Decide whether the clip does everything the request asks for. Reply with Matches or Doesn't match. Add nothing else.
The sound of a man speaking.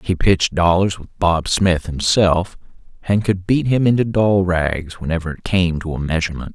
Matches